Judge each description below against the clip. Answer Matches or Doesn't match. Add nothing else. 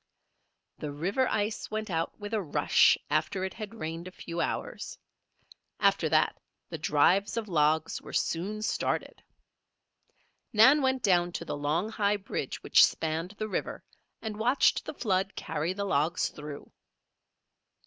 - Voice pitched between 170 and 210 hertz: Matches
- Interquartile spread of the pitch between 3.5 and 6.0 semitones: Matches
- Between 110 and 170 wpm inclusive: Matches